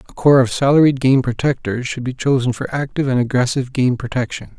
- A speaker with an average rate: Yes, average, 195 wpm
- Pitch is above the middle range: No, low, 125 Hz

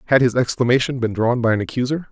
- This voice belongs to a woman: No, male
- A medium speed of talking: No, fast, 225 wpm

